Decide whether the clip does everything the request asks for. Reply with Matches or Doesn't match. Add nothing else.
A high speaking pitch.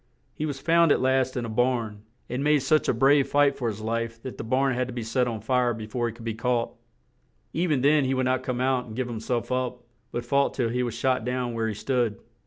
Doesn't match